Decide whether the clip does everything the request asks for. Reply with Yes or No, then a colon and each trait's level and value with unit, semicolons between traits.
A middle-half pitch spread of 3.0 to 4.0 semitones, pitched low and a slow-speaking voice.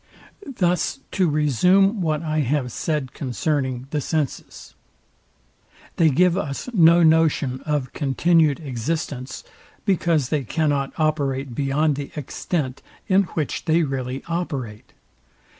No: average, 3.5 semitones; medium, 150 Hz; slow, 115 wpm